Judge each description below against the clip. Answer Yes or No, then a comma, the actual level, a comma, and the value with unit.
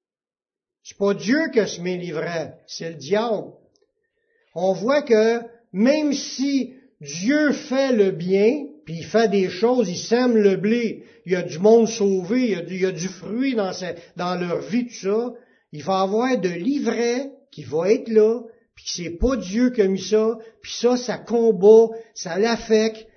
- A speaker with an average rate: Yes, average, 185 wpm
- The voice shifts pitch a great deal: No, average, 4.3 semitones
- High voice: Yes, high, 220 Hz